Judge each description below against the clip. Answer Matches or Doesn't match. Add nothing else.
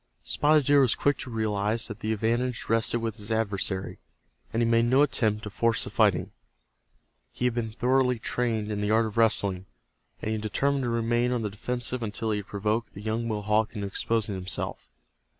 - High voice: Doesn't match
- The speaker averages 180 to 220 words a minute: Matches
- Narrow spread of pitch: Matches